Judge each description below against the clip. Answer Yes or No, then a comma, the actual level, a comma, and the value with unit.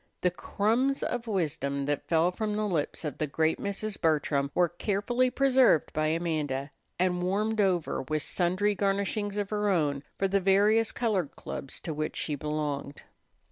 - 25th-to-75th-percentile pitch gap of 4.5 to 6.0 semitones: Yes, average, 5.2 semitones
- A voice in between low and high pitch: Yes, medium, 180 Hz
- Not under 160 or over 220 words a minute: Yes, average, 165 wpm